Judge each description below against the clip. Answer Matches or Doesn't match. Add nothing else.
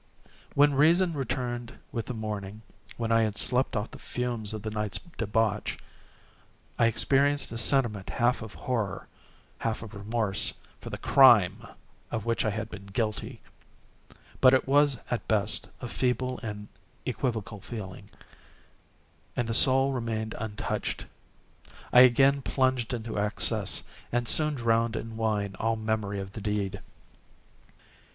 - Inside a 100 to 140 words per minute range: Matches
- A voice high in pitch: Doesn't match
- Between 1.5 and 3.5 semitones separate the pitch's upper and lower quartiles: Matches